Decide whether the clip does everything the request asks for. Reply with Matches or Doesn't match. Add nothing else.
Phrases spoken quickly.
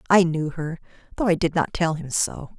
Matches